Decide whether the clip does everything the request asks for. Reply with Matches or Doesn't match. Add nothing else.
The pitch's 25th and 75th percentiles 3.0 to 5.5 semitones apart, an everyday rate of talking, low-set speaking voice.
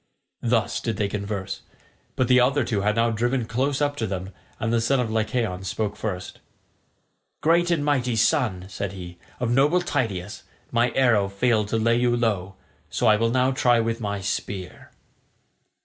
Matches